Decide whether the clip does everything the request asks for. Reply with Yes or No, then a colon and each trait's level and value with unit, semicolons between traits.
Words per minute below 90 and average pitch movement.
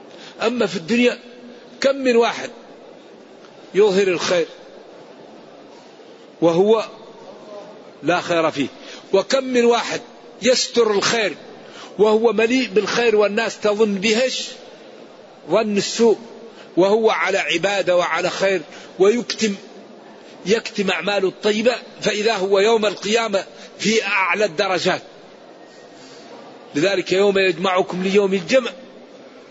No: average, 95 wpm; average, 3.5 semitones